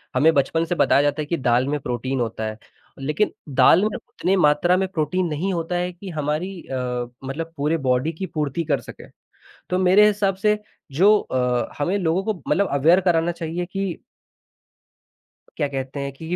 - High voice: No, medium, 160 Hz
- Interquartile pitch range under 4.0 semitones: No, average, 4.7 semitones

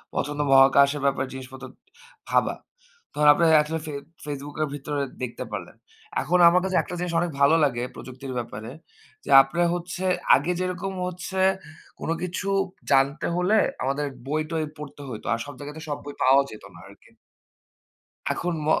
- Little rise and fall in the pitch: No, average, 4.0 semitones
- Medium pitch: Yes, medium, 145 Hz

